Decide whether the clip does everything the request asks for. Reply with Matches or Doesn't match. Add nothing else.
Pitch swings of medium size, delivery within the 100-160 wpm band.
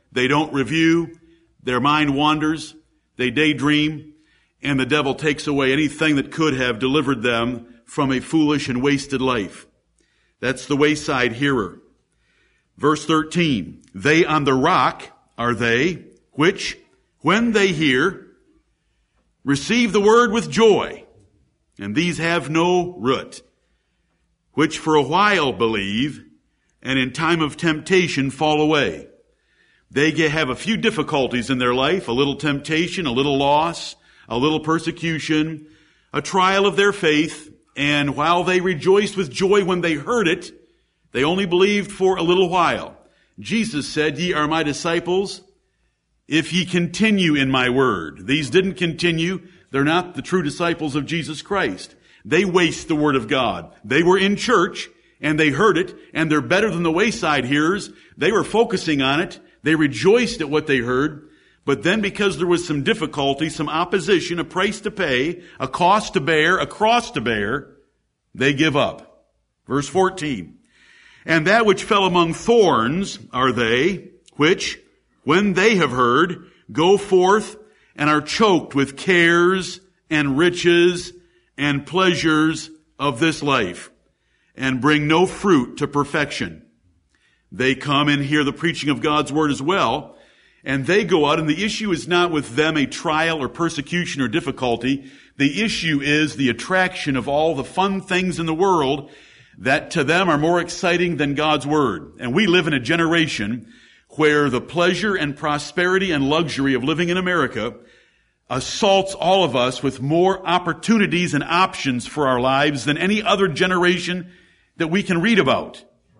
Matches